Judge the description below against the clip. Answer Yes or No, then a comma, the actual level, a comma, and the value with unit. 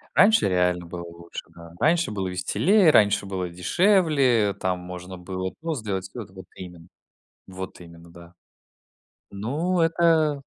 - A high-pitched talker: No, very low, 95 Hz